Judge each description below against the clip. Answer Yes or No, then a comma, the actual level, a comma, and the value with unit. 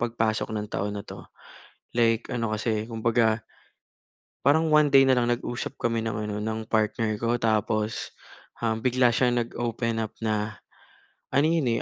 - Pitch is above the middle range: No, low, 115 Hz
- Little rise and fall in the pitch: Yes, narrow, 1.8 semitones